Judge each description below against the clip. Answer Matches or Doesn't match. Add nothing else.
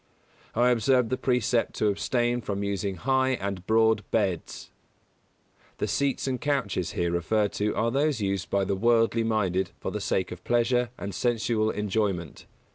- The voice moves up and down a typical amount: Matches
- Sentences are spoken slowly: Doesn't match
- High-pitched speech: Doesn't match